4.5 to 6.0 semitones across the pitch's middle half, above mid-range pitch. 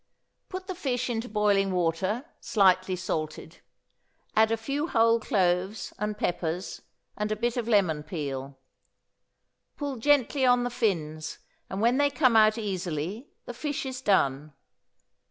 Yes: wide, 5.4 semitones; high, 210 Hz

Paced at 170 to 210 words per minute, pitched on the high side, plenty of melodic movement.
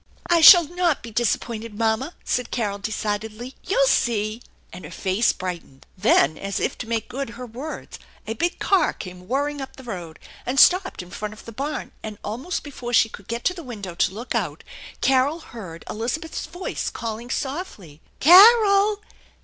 Yes: average, 185 wpm; high, 235 Hz; wide, 6.4 semitones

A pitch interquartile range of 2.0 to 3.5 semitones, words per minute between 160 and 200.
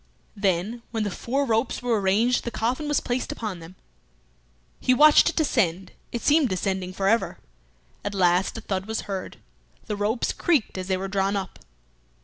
No: average, 4.2 semitones; average, 175 wpm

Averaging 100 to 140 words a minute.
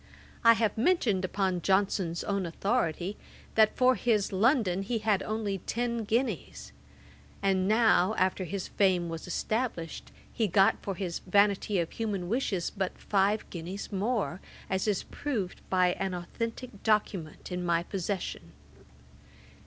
Yes: slow, 135 wpm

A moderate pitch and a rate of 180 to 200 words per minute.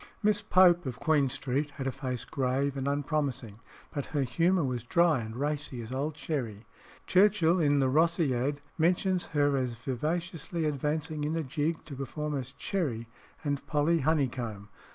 No: medium, 145 Hz; average, 160 wpm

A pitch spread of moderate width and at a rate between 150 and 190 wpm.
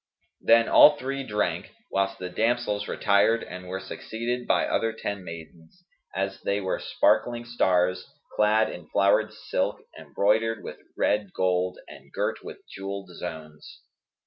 No: average, 3.7 semitones; average, 140 wpm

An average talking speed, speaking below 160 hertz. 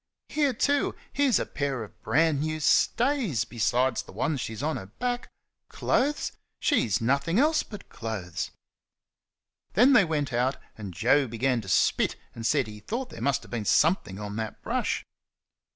Yes: average, 165 wpm; medium, 140 Hz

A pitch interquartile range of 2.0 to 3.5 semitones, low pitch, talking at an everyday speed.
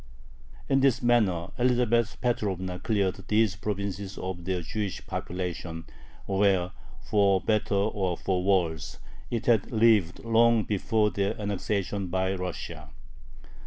No: average, 2.9 semitones; low, 100 Hz; slow, 120 wpm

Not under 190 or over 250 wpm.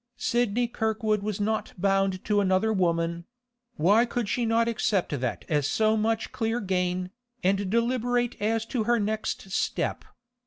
No: average, 150 wpm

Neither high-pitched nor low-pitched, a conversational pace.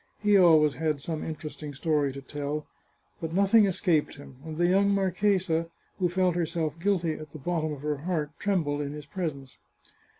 Yes: medium, 160 Hz; average, 175 wpm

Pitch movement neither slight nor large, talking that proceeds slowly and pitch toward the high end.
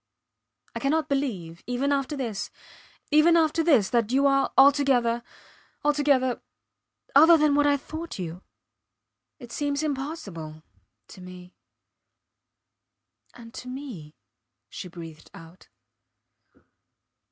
No: wide, 7.0 semitones; slow, 105 wpm; very high, 265 Hz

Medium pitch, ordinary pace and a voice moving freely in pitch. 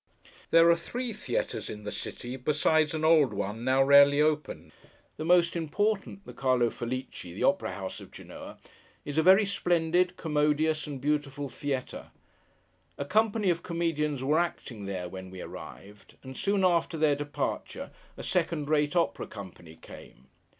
No: medium, 150 Hz; average, 150 wpm; average, 4.7 semitones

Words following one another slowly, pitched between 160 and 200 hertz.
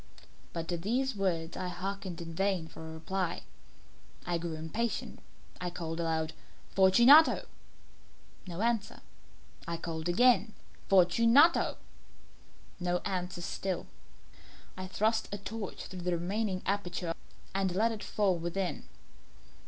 Yes: slow, 125 wpm; medium, 185 Hz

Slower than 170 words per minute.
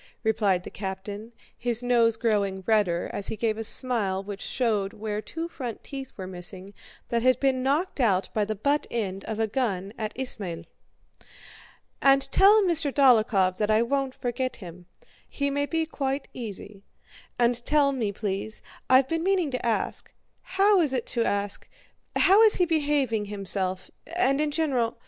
Yes: average, 150 wpm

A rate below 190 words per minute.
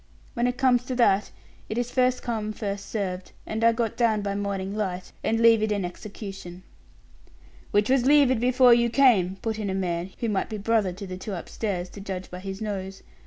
No: fast, 205 wpm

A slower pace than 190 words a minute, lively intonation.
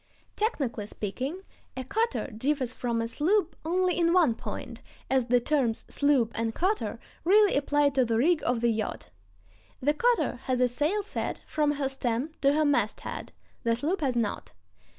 Yes: average, 170 wpm; wide, 5.8 semitones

